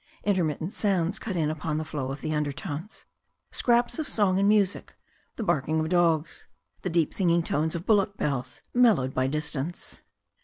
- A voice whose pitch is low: No, medium, 165 Hz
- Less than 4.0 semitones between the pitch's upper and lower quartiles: No, average, 4.7 semitones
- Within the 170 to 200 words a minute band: Yes, average, 180 wpm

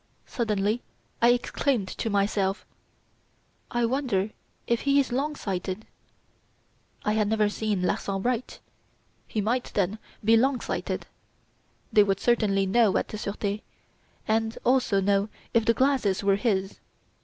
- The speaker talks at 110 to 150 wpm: Yes, slow, 135 wpm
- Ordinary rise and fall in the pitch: Yes, average, 3.3 semitones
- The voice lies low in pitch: No, high, 215 Hz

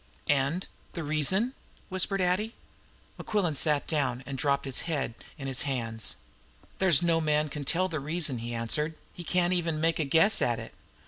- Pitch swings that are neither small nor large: Yes, average, 4.3 semitones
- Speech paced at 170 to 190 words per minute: Yes, average, 175 wpm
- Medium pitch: Yes, medium, 155 Hz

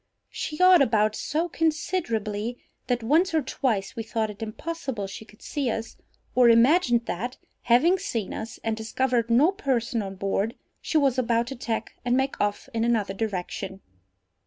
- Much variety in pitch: No, average, 4.0 semitones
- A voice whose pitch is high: Yes, high, 235 Hz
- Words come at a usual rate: Yes, average, 165 wpm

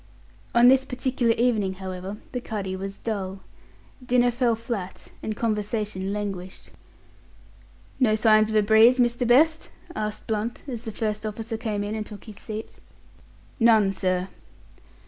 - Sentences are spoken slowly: No, average, 145 wpm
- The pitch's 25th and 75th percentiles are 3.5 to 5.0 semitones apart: No, average, 2.7 semitones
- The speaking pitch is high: Yes, high, 215 Hz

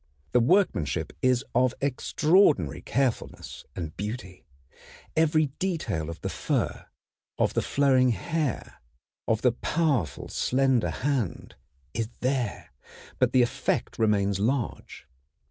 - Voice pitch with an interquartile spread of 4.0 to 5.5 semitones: Yes, average, 5.0 semitones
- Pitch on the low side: Yes, low, 125 Hz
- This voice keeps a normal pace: No, slow, 110 wpm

